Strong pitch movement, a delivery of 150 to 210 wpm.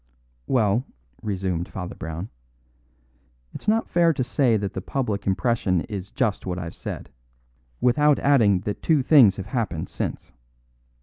No: wide, 5.7 semitones; average, 140 wpm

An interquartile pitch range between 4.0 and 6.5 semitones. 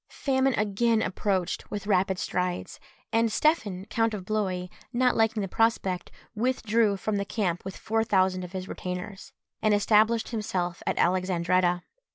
No: average, 3.4 semitones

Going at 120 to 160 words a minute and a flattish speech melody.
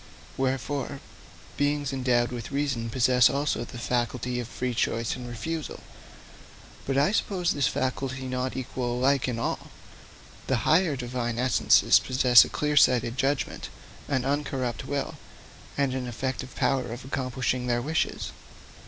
Yes: average, 140 wpm; narrow, 2.2 semitones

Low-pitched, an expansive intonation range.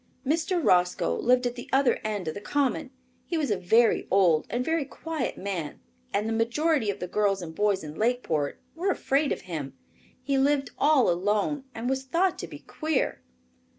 No: high, 240 Hz; wide, 7.0 semitones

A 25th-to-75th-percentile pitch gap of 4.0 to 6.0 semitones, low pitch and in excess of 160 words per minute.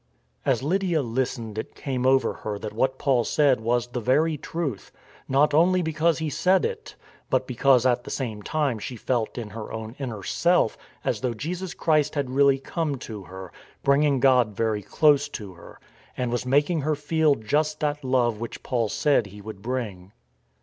Yes: average, 4.8 semitones; low, 130 Hz; average, 185 wpm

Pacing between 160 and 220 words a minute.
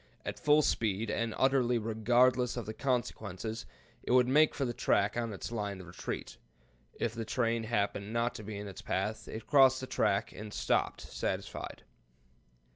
Yes: average, 175 wpm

